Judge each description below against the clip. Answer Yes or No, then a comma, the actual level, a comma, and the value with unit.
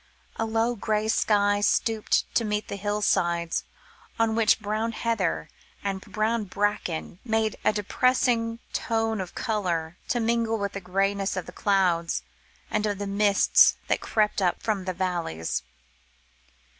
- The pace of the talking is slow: No, average, 145 wpm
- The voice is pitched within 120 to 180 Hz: No, high, 210 Hz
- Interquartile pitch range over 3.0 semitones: No, average, 2.7 semitones